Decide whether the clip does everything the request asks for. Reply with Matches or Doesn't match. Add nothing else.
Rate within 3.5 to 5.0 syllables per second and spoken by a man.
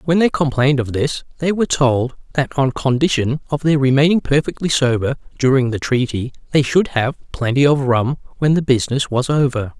Doesn't match